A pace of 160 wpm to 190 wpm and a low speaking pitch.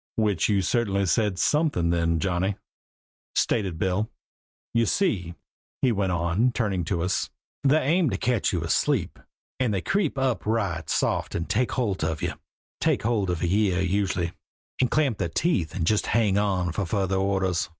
Yes: average, 170 wpm; low, 100 Hz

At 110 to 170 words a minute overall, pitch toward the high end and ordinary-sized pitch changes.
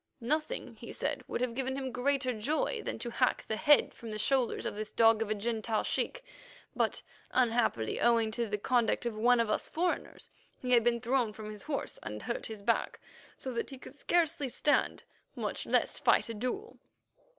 No: average, 195 wpm; high, 240 Hz; average, 3.4 semitones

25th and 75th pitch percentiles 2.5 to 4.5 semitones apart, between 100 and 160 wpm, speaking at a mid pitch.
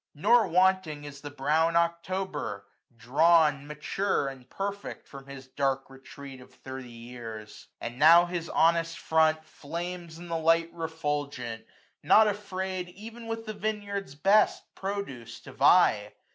No: average, 5.3 semitones; average, 140 wpm; medium, 160 Hz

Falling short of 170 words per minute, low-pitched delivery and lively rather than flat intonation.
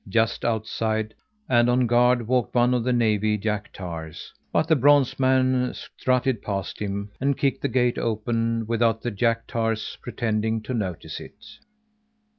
No: average, 155 wpm; low, 115 Hz; narrow, 2.6 semitones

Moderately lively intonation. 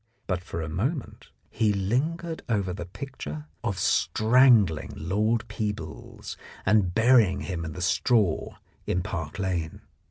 Yes: average, 4.9 semitones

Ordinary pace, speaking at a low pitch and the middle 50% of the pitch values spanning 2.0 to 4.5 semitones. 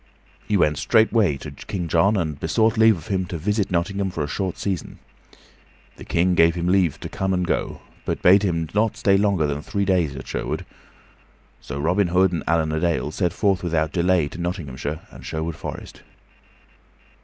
Yes: average, 195 wpm; very low, 90 Hz; average, 3.4 semitones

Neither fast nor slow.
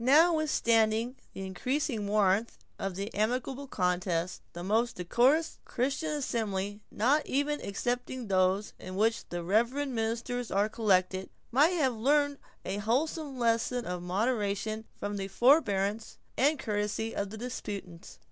No: slow, 130 wpm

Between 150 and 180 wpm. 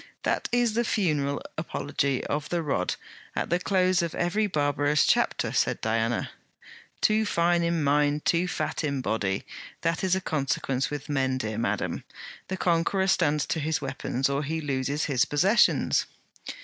Yes: average, 160 wpm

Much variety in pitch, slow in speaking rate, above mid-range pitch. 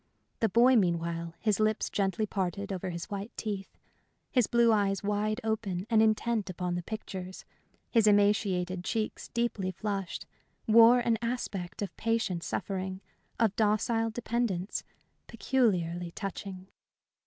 No: average, 3.4 semitones; slow, 130 wpm; high, 205 Hz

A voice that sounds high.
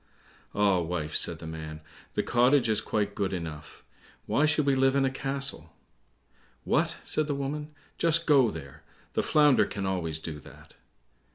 No: low, 110 Hz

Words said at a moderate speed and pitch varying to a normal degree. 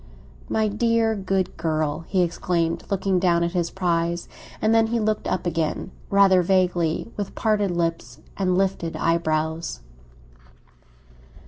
No: slow, 130 wpm; average, 3.0 semitones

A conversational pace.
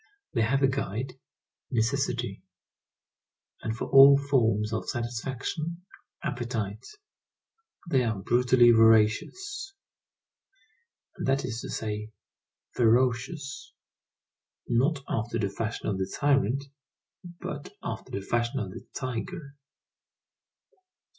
No: slow, 100 wpm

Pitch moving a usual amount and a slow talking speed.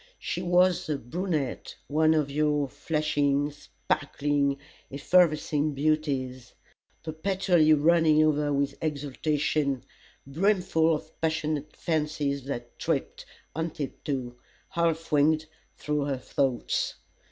No: narrow, 2.2 semitones; slow, 100 wpm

